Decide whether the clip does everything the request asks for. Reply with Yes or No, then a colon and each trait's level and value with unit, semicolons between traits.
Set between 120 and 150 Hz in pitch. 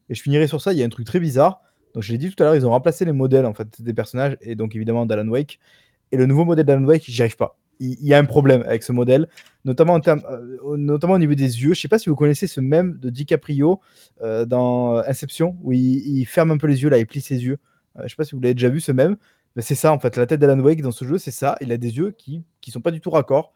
Yes: medium, 140 Hz